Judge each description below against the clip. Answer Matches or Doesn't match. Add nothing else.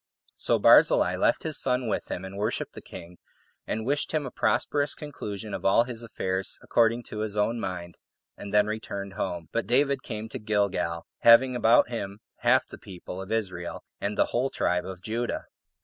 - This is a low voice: Matches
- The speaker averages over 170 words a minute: Matches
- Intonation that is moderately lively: Matches